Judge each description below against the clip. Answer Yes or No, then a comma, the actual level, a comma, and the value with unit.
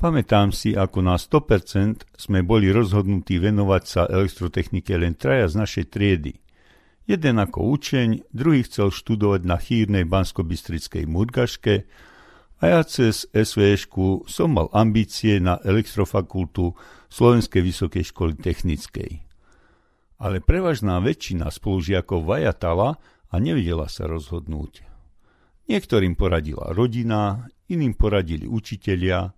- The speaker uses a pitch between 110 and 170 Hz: No, low, 100 Hz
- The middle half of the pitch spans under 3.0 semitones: No, average, 3.6 semitones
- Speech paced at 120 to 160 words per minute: No, slow, 110 wpm